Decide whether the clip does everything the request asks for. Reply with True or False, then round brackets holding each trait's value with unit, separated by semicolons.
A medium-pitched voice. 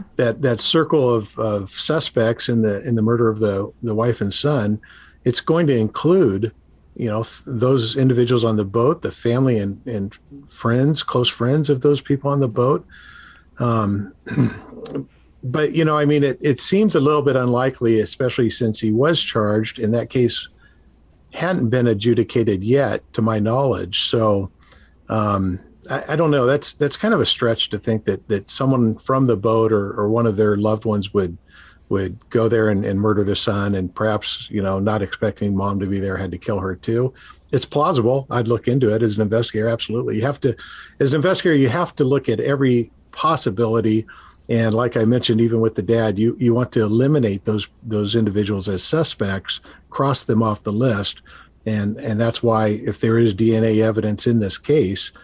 False (115 Hz)